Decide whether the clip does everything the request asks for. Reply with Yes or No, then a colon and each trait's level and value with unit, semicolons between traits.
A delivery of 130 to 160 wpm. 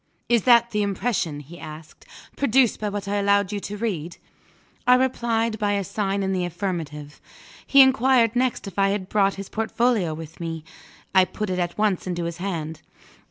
No: average, 185 wpm